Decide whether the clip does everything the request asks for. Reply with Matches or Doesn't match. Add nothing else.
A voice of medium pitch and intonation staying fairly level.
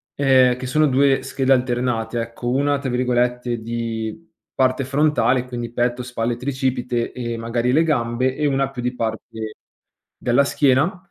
Doesn't match